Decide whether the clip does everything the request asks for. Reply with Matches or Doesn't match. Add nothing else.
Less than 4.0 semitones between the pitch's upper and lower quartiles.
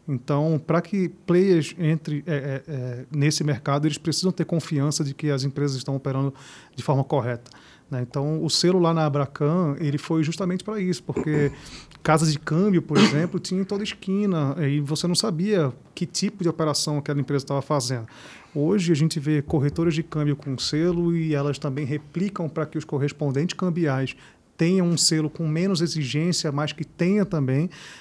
Matches